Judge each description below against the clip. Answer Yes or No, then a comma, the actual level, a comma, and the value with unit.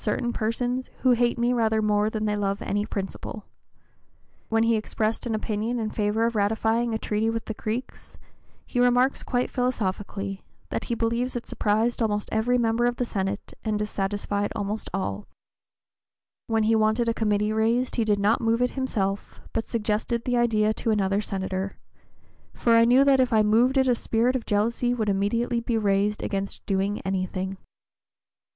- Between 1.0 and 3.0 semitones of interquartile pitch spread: Yes, narrow, 2.4 semitones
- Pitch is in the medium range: No, high, 220 Hz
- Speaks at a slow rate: No, average, 175 wpm